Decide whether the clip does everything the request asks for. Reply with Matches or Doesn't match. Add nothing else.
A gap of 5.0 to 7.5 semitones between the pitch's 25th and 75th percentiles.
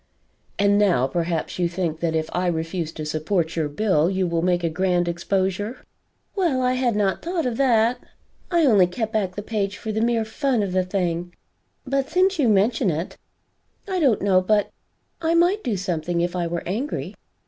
Matches